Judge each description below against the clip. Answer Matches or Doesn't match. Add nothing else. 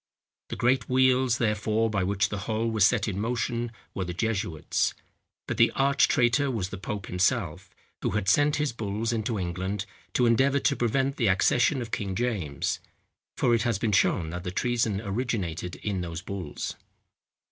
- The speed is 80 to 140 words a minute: Doesn't match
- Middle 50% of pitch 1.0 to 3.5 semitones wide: Doesn't match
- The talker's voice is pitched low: Matches